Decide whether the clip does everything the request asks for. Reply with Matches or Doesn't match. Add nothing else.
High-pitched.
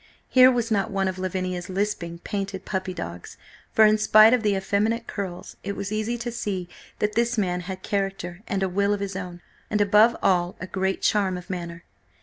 Matches